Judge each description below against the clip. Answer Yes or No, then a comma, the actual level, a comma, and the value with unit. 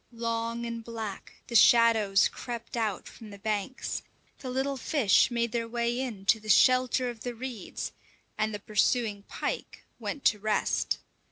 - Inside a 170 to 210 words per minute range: No, average, 160 wpm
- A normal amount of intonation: No, narrow, 2.3 semitones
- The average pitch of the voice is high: Yes, high, 230 Hz